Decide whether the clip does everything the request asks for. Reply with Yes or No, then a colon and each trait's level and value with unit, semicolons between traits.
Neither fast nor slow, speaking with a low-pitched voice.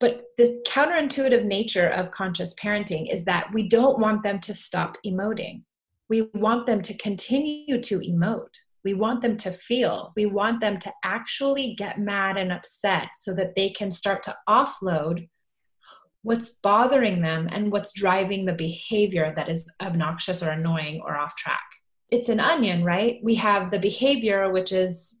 No: average, 165 wpm; high, 205 Hz